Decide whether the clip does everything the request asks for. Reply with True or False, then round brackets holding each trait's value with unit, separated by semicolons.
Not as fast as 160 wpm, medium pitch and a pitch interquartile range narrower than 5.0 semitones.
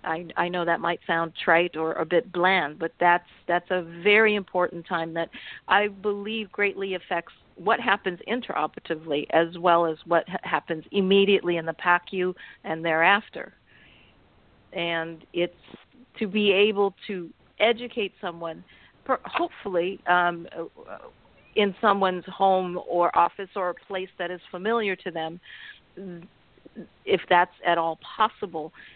True (135 wpm; 180 Hz; 2.8 semitones)